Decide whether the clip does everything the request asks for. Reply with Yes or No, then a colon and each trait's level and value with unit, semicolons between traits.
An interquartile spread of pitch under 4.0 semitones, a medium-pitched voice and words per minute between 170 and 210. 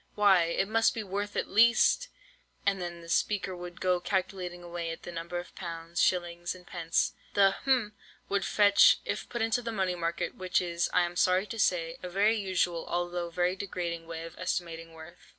Yes: average, 2.7 semitones; medium, 180 Hz; average, 185 wpm